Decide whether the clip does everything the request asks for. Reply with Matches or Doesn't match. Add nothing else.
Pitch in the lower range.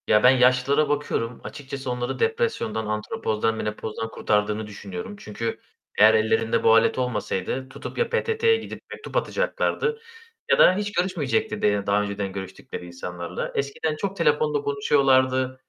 Matches